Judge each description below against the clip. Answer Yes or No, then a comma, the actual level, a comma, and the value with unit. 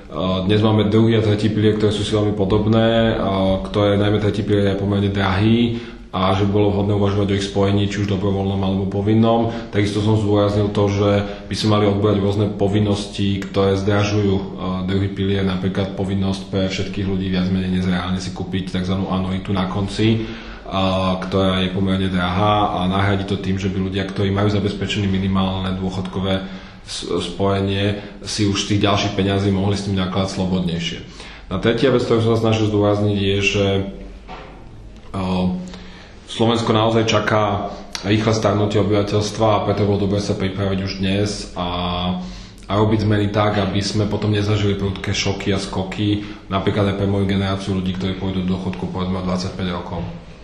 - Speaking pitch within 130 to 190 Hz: No, low, 100 Hz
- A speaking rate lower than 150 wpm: No, fast, 165 wpm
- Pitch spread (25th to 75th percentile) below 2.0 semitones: Yes, narrow, 1.5 semitones